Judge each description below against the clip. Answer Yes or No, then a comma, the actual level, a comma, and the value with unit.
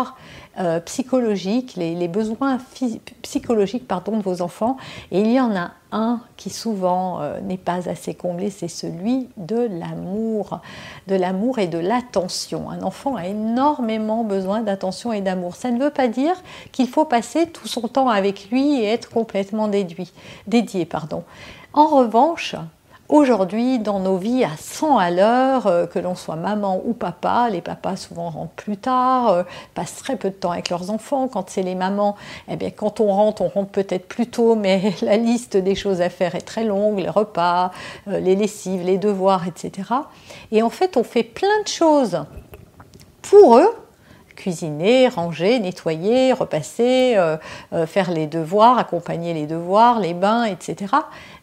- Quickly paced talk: No, average, 165 wpm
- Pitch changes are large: No, average, 4.7 semitones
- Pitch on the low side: No, high, 210 Hz